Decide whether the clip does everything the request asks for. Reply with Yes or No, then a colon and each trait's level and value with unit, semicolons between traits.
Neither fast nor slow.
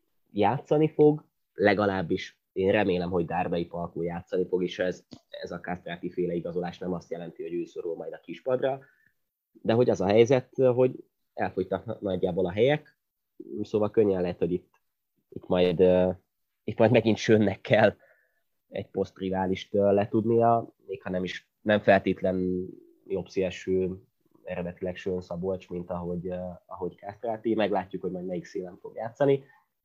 Yes: average, 145 wpm